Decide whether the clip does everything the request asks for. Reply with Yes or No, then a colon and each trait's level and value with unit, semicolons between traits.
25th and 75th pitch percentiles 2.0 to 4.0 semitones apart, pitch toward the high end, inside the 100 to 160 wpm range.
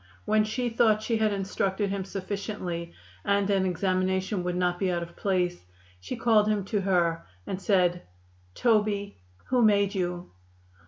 Yes: average, 2.7 semitones; high, 195 Hz; average, 155 wpm